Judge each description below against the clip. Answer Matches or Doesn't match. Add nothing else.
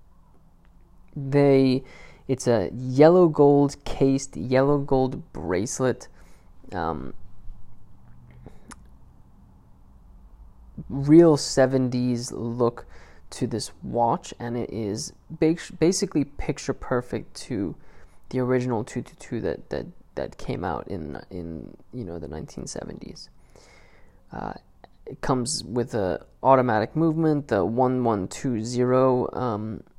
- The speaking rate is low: Matches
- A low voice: Matches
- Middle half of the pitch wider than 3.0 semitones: Matches